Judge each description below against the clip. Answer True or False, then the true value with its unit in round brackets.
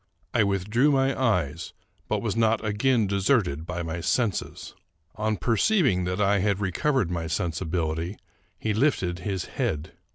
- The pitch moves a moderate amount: True (4.6 semitones)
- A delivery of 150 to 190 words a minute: False (140 wpm)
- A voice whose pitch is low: True (100 Hz)